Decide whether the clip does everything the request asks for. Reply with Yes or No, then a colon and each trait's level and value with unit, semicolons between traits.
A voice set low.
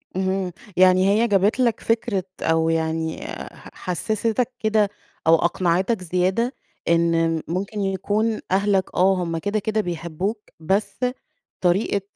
No: high, 190 Hz